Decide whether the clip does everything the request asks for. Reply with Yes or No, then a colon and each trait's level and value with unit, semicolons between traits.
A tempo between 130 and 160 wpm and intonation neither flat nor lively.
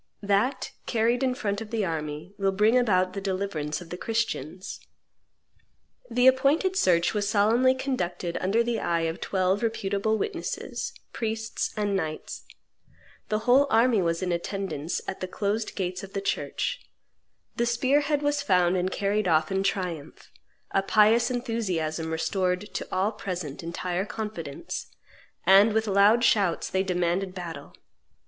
Yes: average, 150 wpm; average, 4.0 semitones